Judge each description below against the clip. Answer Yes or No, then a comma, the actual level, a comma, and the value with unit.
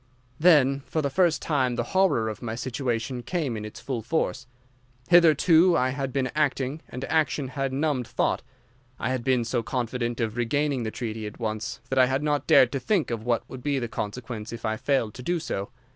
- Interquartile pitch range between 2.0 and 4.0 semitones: Yes, average, 3.7 semitones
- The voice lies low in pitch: Yes, low, 130 Hz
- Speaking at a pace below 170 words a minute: No, fast, 205 wpm